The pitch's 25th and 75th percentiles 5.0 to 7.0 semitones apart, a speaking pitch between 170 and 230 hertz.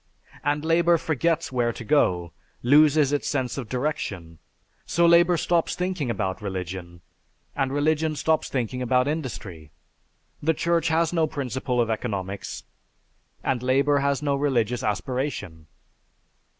No: wide, 5.5 semitones; low, 135 Hz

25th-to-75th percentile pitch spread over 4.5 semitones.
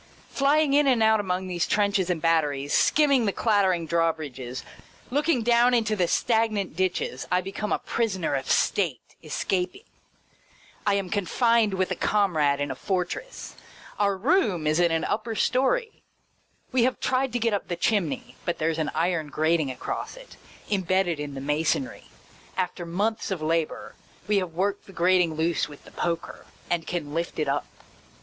Yes: average, 5.3 semitones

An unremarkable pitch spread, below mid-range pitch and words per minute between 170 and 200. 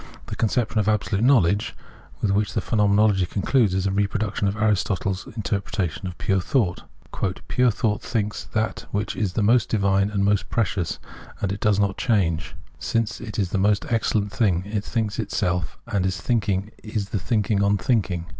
No: narrow, 2.0 semitones; low, 100 Hz; average, 185 wpm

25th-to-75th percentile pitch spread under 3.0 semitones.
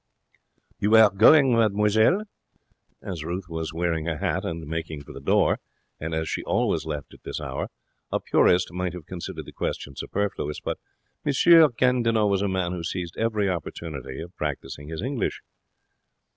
No: average, 4.6 semitones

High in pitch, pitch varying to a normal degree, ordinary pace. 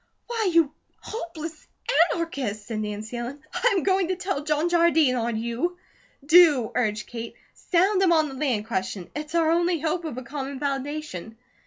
No: very high, 300 Hz; wide, 6.2 semitones; average, 170 wpm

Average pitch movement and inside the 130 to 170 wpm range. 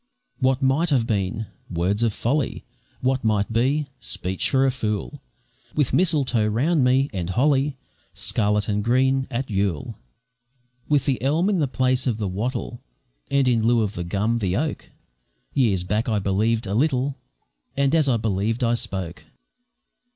Yes: average, 4.5 semitones; average, 160 wpm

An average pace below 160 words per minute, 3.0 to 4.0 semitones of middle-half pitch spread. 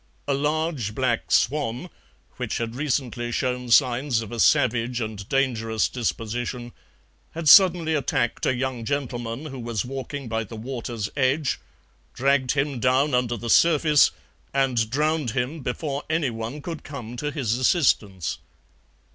Yes: average, 140 wpm; average, 3.5 semitones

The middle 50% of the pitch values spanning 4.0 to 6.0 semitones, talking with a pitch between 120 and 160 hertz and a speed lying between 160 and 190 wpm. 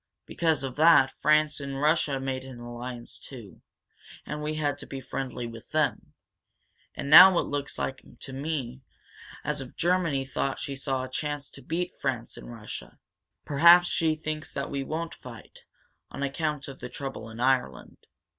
No: average, 2.9 semitones; medium, 140 Hz; average, 165 wpm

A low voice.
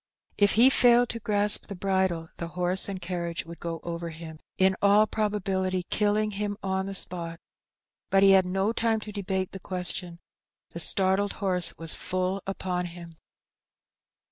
No: high, 190 Hz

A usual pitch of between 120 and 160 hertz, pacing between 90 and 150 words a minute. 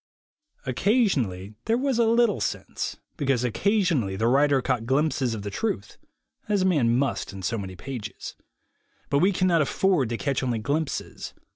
No: low, 135 Hz; average, 165 wpm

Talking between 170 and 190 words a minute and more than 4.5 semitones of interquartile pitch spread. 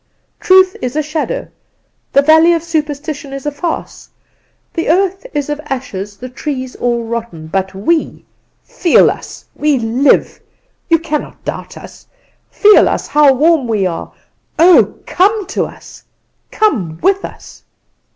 No: average, 140 wpm; wide, 5.5 semitones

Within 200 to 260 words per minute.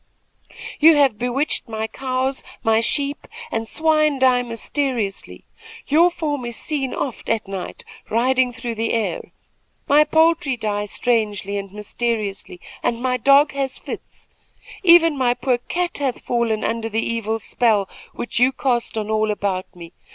No: average, 150 wpm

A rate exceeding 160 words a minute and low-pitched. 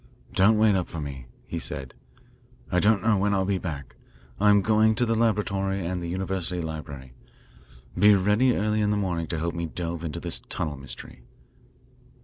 Yes: average, 180 wpm; very low, 95 Hz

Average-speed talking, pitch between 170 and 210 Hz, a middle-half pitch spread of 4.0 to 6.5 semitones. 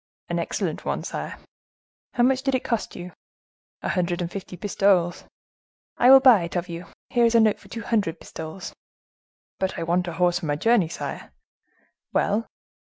Yes: average, 180 wpm; medium, 185 Hz; average, 5.0 semitones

